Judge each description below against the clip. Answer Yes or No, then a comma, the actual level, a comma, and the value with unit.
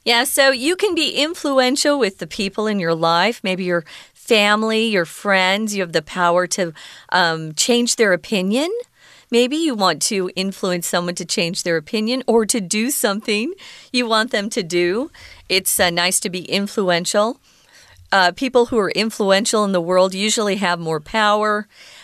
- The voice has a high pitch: Yes, high, 210 Hz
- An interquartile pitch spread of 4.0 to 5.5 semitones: Yes, average, 4.6 semitones